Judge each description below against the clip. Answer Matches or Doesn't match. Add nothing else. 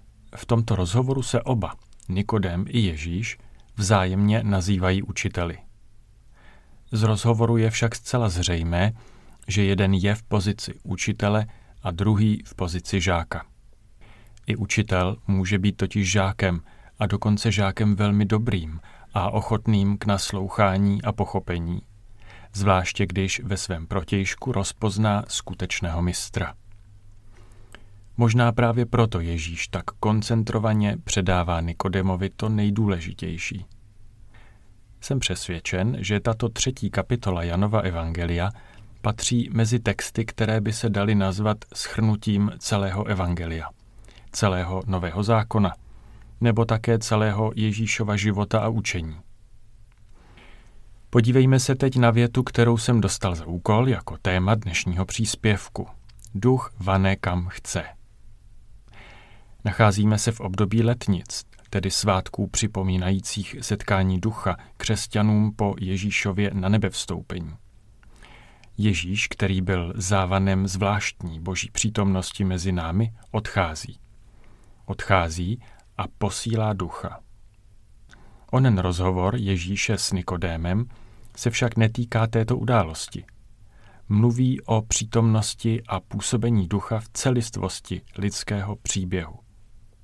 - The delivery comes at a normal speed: Doesn't match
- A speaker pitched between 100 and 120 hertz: Matches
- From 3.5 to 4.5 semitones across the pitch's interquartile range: Doesn't match